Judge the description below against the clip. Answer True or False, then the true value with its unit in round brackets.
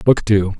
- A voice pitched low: True (105 Hz)